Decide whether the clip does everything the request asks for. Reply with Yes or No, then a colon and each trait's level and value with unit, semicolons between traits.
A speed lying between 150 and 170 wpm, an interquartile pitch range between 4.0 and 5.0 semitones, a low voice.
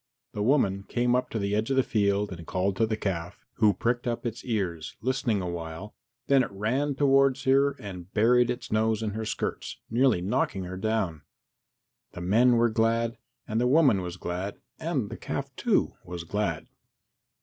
No: average, 185 wpm; average, 4.3 semitones; low, 110 Hz